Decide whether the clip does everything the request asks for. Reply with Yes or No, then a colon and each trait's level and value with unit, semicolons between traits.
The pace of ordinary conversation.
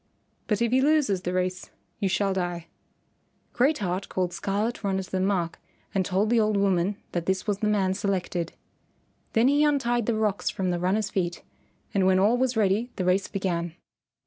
Yes: average, 190 wpm